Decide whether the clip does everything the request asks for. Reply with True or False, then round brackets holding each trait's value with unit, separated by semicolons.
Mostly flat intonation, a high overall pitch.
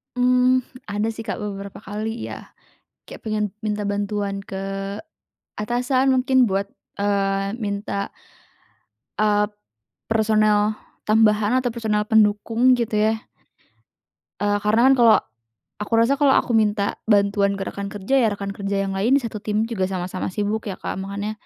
True (2.0 semitones; 210 Hz)